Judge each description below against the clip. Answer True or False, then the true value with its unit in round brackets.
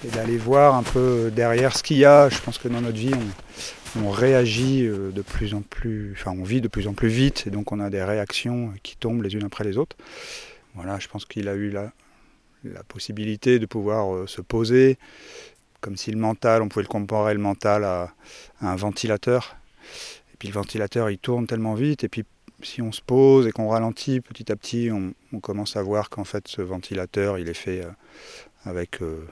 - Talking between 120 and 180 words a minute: False (220 wpm)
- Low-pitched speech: True (110 Hz)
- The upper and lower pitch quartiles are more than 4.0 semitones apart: False (3.2 semitones)